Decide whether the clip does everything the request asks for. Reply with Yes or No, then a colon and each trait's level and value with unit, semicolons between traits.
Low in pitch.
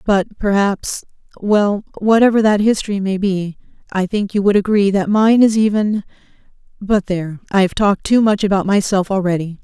No: high, 200 Hz